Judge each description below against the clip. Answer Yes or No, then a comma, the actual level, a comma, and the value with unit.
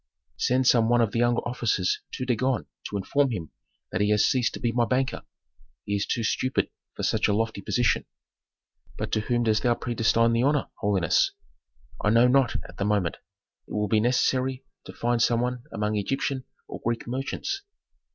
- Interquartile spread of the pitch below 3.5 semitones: Yes, average, 3.0 semitones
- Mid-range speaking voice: No, low, 120 Hz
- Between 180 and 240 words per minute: Yes, average, 190 wpm